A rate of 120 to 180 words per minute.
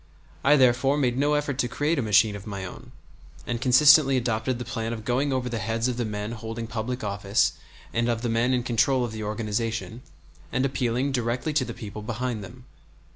No: fast, 205 wpm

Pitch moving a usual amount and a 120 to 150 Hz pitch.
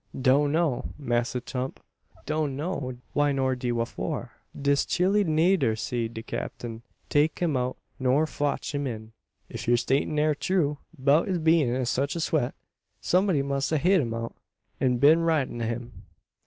Yes: average, 4.0 semitones; medium, 140 Hz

